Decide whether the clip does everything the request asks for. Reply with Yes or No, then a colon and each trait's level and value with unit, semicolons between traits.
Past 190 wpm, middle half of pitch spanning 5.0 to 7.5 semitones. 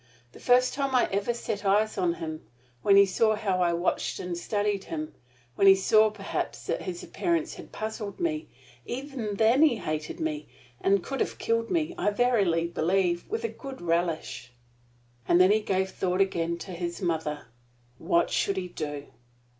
No: average, 180 wpm; wide, 5.4 semitones